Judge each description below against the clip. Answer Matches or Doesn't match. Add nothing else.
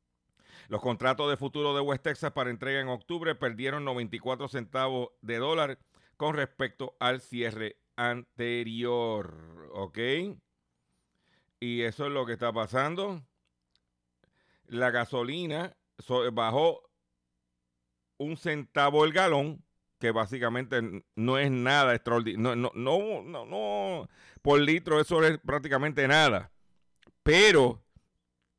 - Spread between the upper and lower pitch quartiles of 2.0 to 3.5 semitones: Doesn't match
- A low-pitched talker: Matches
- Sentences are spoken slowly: Matches